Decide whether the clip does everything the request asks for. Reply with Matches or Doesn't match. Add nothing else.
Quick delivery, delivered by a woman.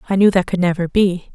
Matches